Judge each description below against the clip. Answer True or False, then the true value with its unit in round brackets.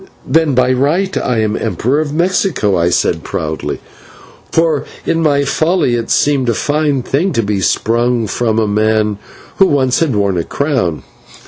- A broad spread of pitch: True (5.8 semitones)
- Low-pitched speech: True (125 Hz)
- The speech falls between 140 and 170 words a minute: True (160 wpm)